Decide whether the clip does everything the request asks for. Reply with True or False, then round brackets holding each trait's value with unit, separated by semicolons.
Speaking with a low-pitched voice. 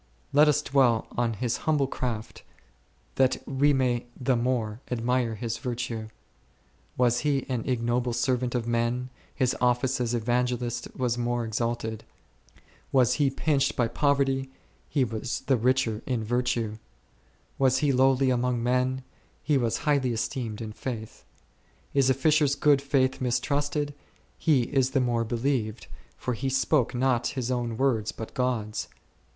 True (125 Hz)